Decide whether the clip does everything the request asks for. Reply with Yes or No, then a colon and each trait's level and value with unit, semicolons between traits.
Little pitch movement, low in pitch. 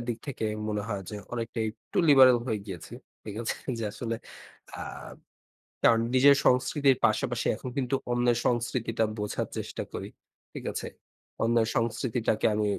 Yes: narrow, 2.3 semitones; low, 115 Hz